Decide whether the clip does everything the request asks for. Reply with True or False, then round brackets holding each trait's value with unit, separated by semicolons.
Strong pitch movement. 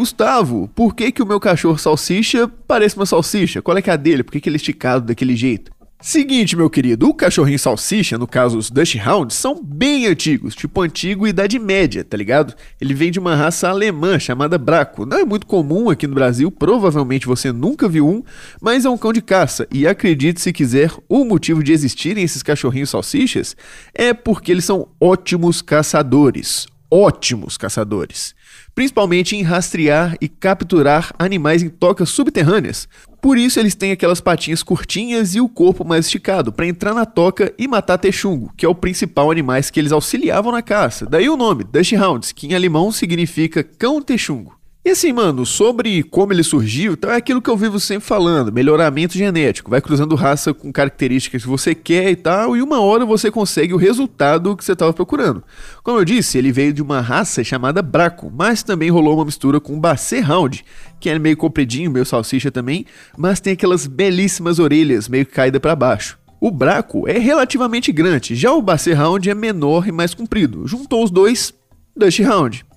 True (5.7 semitones)